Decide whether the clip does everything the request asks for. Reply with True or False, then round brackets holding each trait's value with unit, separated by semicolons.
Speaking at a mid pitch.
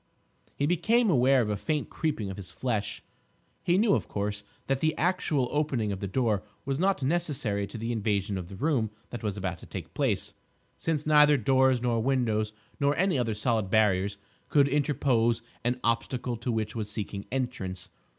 False (120 Hz)